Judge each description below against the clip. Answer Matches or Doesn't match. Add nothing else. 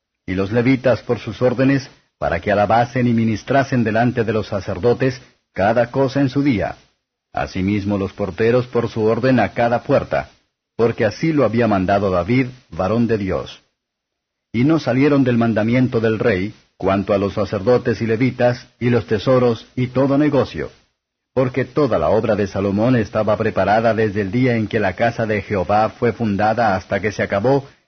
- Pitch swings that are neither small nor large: Matches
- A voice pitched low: Matches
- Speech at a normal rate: Matches